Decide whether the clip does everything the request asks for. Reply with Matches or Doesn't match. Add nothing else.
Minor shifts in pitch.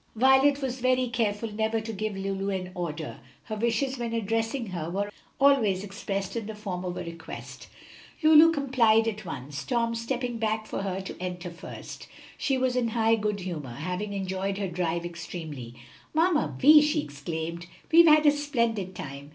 Doesn't match